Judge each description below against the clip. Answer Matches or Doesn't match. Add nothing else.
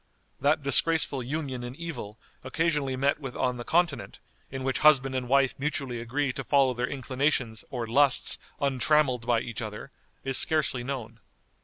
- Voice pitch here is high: Doesn't match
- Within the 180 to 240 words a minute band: Doesn't match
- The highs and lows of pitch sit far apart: Doesn't match